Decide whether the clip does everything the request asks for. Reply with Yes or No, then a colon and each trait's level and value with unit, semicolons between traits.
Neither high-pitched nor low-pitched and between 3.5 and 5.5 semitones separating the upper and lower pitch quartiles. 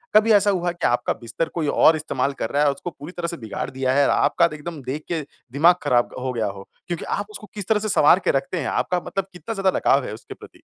Yes: medium, 155 Hz; average, 5.2 semitones